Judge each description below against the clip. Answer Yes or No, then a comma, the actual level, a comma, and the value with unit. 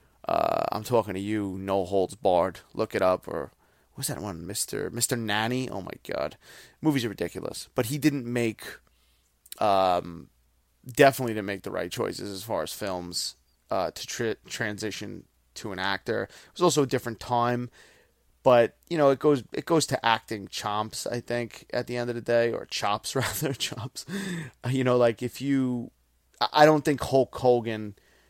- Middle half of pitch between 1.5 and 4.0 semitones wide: No, average, 4.7 semitones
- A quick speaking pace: No, average, 180 wpm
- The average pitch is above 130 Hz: No, low, 120 Hz